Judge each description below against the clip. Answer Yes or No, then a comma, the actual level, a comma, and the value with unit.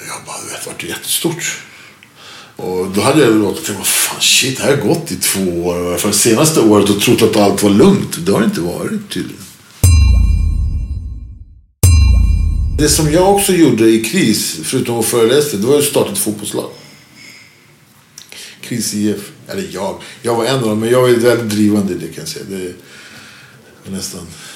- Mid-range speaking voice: No, low, 100 Hz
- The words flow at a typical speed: Yes, average, 165 wpm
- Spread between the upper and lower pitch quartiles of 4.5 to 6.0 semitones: Yes, average, 4.9 semitones